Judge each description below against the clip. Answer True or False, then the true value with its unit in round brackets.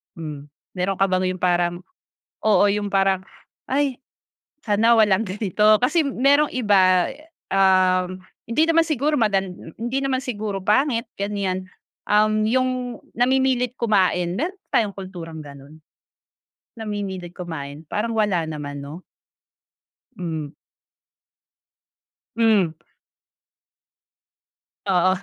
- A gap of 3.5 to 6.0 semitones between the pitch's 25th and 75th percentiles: True (4.4 semitones)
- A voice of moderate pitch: False (200 Hz)